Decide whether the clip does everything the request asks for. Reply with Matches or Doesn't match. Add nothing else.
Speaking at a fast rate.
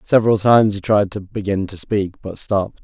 Matches